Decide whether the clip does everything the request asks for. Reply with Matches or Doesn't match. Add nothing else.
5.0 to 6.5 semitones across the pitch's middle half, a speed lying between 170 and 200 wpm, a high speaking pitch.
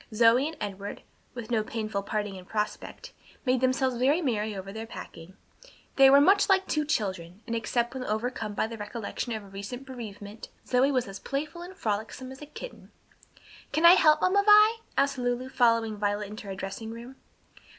Doesn't match